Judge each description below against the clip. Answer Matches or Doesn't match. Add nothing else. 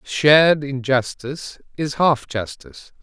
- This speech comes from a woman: Doesn't match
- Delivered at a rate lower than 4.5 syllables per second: Matches